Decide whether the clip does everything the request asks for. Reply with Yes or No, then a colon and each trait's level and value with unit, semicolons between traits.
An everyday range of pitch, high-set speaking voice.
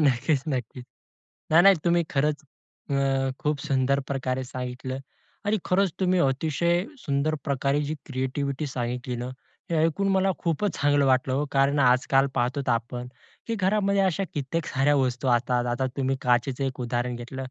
No: average, 3.4 semitones; low, 135 Hz